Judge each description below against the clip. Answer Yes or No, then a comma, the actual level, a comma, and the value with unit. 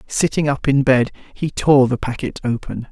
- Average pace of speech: Yes, average, 185 wpm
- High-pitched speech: No, low, 135 Hz